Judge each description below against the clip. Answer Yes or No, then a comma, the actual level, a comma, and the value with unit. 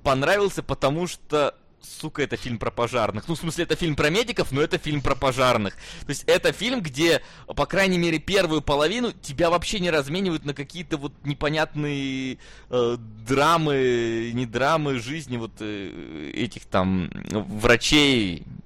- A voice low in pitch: No, medium, 145 Hz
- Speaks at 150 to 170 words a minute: Yes, average, 155 wpm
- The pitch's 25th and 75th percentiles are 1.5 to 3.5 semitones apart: No, average, 5.2 semitones